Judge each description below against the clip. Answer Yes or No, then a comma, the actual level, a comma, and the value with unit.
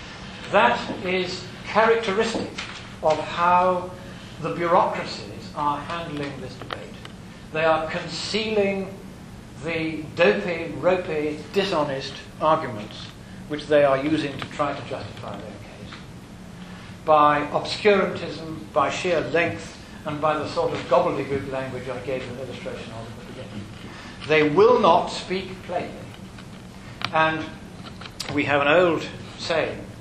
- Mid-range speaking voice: Yes, medium, 155 Hz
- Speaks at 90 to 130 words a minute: Yes, average, 120 wpm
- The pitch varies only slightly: No, average, 5.0 semitones